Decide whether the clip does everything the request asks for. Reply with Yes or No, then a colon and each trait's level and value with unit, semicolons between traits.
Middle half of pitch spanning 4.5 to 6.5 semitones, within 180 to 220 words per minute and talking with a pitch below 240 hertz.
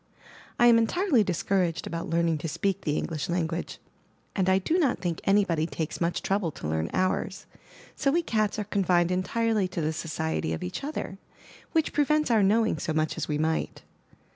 Yes: average, 5.2 semitones; average, 190 wpm; medium, 185 Hz